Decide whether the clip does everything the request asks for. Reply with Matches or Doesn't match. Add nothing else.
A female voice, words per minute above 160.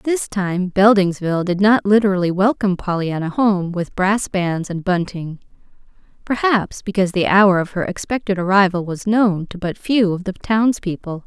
Doesn't match